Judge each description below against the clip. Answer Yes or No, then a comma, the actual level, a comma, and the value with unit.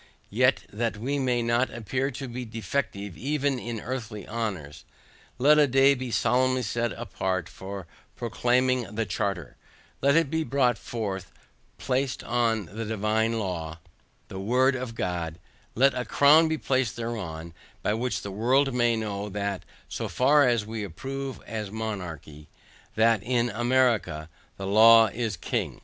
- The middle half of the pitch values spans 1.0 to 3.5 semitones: No, average, 4.1 semitones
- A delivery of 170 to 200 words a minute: No, average, 150 wpm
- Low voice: Yes, low, 115 Hz